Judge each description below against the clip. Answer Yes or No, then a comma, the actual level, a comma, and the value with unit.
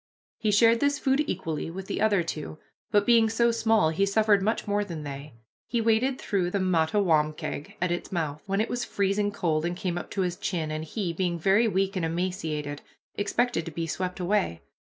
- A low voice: No, high, 190 Hz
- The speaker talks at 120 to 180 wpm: No, average, 200 wpm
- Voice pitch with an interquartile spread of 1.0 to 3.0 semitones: No, average, 4.5 semitones